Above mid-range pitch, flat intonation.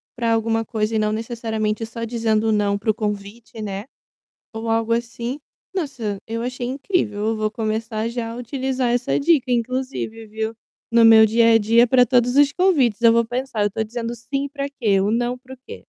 Yes: high, 230 Hz; narrow, 2.2 semitones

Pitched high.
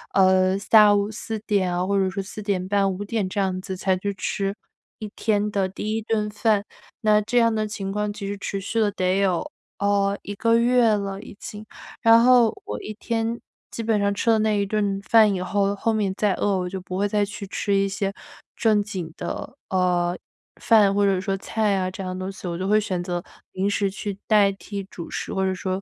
Yes: high, 200 Hz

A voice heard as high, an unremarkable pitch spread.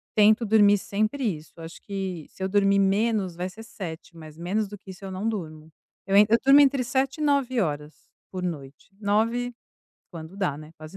Yes: high, 195 Hz; average, 4.8 semitones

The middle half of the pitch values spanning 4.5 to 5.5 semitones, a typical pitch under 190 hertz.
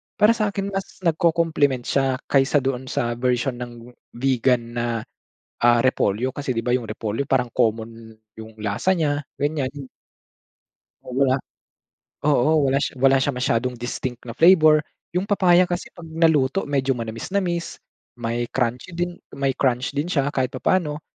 Yes: average, 4.8 semitones; low, 135 Hz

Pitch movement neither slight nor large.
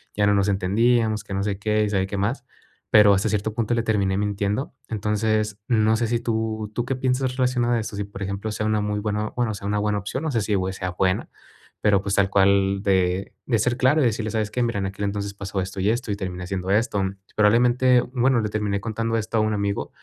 No: narrow, 2.3 semitones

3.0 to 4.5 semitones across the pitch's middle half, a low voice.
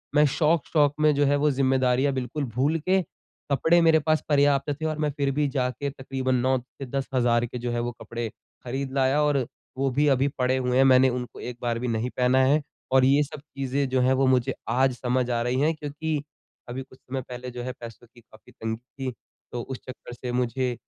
No: narrow, 2.4 semitones; low, 130 Hz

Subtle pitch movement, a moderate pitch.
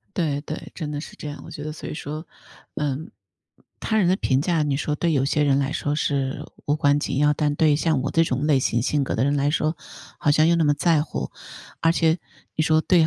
Yes: narrow, 1.9 semitones; medium, 150 Hz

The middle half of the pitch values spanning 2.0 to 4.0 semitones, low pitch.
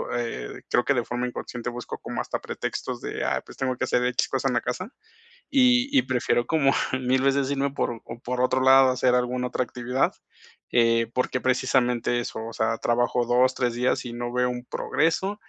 No: narrow, 1.5 semitones; low, 125 Hz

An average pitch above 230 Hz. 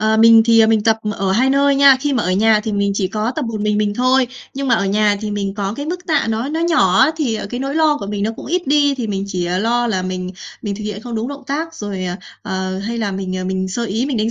No: high, 220 Hz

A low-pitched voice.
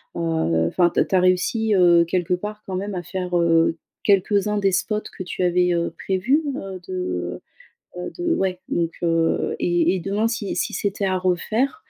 No: medium, 185 Hz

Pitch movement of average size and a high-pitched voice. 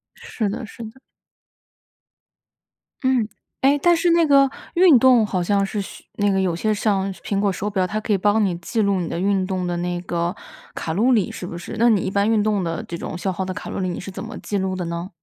Yes: average, 3.3 semitones; high, 200 Hz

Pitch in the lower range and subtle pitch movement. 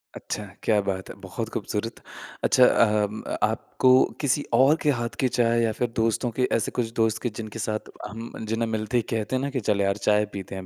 Yes: low, 110 Hz; narrow, 2.1 semitones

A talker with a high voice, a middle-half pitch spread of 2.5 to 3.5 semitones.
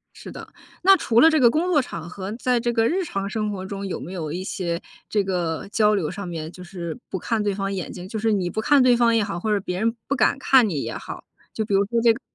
No: high, 205 Hz; average, 4.2 semitones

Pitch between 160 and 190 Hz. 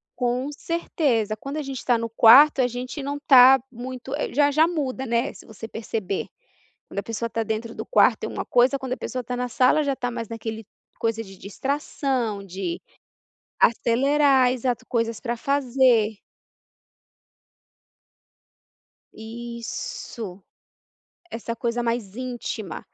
No: high, 240 Hz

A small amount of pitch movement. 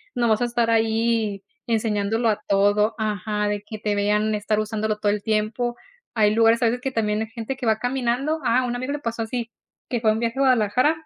Yes: narrow, 2.2 semitones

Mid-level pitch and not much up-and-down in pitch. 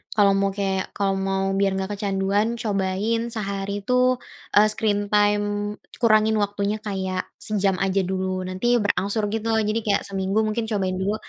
No: high, 205 Hz; narrow, 1.9 semitones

